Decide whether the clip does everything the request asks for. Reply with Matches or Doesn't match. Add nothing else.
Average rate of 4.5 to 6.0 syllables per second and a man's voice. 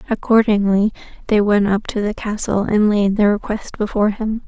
Doesn't match